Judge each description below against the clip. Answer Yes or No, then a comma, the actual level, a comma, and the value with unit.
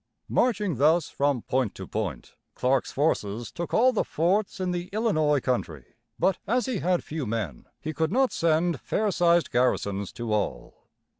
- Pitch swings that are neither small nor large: No, wide, 7.6 semitones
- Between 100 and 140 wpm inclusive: No, average, 165 wpm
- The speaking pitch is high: No, medium, 155 Hz